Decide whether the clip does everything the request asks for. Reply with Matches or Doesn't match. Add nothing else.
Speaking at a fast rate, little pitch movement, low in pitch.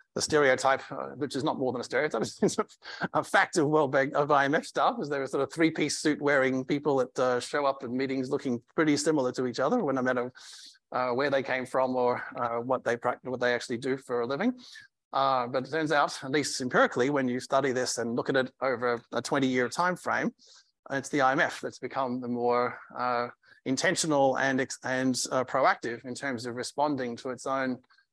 Matches